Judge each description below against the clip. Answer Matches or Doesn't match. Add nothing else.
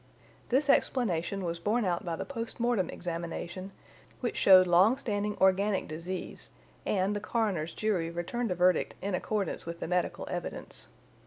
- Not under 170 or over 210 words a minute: Doesn't match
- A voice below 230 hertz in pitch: Matches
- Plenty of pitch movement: Doesn't match